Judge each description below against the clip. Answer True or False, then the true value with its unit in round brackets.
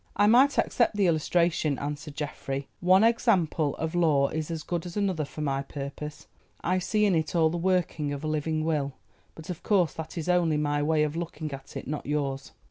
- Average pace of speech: False (210 wpm)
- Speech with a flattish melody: False (3.2 semitones)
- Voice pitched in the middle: True (160 Hz)